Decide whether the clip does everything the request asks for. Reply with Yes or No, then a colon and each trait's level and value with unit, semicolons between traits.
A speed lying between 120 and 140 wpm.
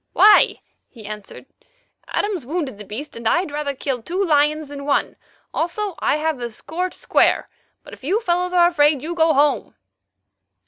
No: average, 175 wpm